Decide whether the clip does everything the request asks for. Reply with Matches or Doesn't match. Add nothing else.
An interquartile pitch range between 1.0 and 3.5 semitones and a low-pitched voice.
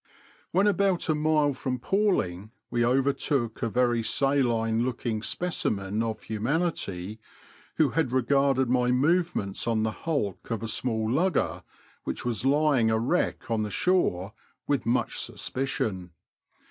Doesn't match